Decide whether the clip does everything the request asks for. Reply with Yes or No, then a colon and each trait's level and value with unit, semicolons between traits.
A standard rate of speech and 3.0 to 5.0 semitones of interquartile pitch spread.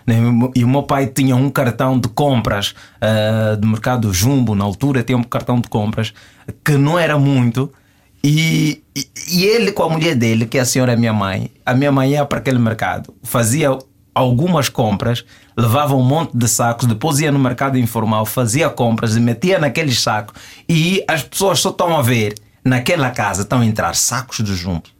No: fast, 190 wpm; average, 3.8 semitones